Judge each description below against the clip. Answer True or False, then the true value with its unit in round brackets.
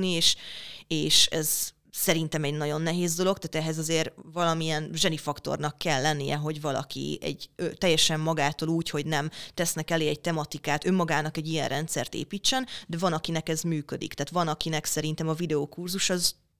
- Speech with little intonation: True (1.9 semitones)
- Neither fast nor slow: False (165 wpm)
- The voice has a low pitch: False (160 Hz)